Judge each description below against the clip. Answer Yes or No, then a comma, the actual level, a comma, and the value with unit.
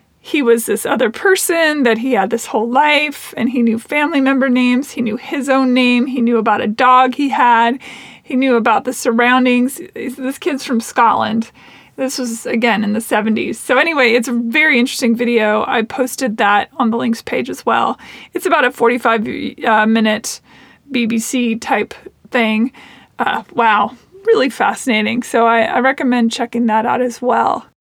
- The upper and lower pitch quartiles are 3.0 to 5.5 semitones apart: No, narrow, 2.4 semitones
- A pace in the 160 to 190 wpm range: Yes, average, 175 wpm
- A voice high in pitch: Yes, high, 245 Hz